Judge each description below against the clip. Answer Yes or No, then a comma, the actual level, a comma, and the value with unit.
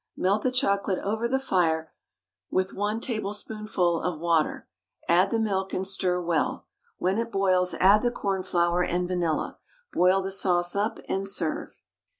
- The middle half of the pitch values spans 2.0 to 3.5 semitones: Yes, narrow, 2.6 semitones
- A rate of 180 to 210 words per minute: No, average, 155 wpm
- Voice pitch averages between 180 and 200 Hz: Yes, high, 190 Hz